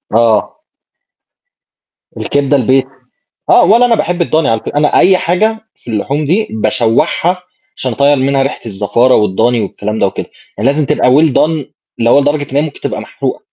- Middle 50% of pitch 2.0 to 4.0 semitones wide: No, wide, 5.4 semitones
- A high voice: No, medium, 140 Hz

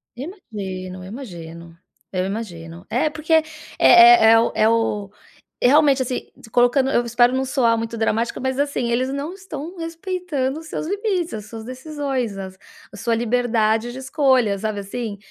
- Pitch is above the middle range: Yes, high, 245 Hz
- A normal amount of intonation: Yes, average, 5.0 semitones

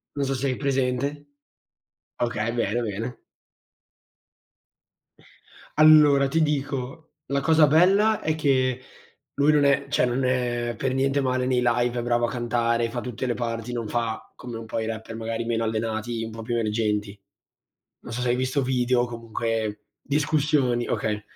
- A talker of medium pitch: No, low, 120 Hz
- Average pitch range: Yes, average, 3.0 semitones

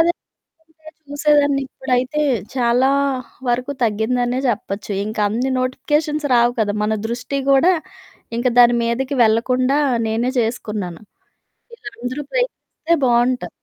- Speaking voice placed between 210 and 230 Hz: No, very high, 250 Hz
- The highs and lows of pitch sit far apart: No, average, 3.4 semitones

